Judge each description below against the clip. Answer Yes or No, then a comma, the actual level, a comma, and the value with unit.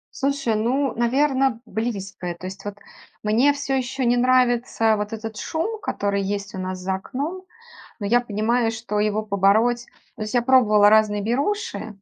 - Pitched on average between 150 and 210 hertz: No, high, 225 Hz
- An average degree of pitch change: Yes, average, 3.7 semitones